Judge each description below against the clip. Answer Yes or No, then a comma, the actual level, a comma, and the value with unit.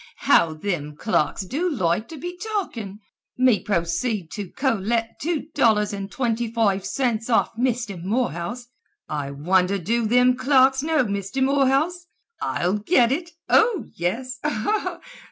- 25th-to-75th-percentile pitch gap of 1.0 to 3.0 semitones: No, wide, 5.4 semitones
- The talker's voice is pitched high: Yes, high, 230 Hz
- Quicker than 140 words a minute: No, slow, 135 wpm